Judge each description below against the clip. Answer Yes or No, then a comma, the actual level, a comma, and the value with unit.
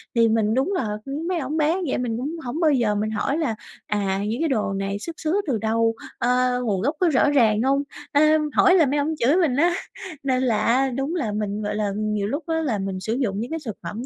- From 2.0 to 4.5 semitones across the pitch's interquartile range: No, wide, 5.6 semitones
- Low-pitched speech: No, very high, 250 Hz